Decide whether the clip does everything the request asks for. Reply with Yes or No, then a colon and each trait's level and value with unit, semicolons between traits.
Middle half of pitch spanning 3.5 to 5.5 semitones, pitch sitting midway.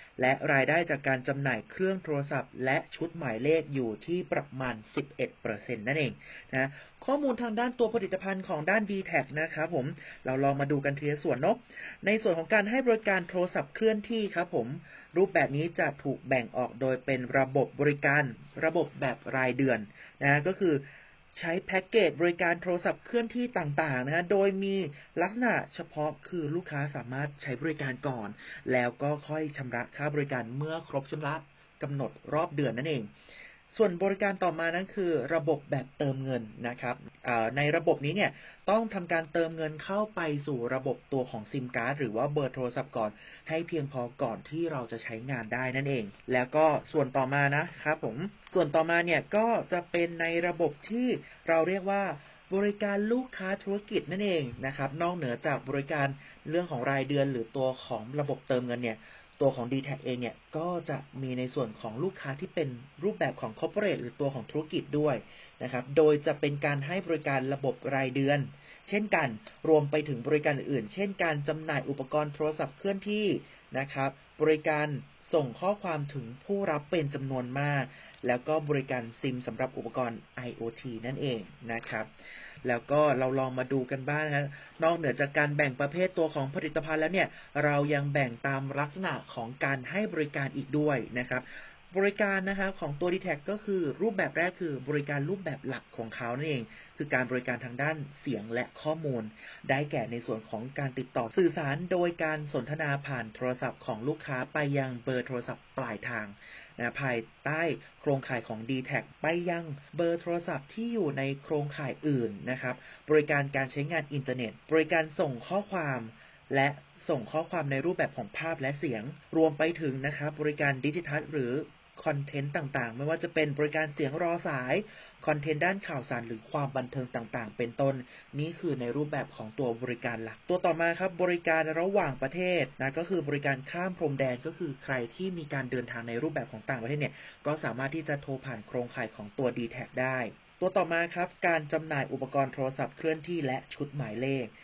Yes: average, 4.1 semitones; medium, 145 Hz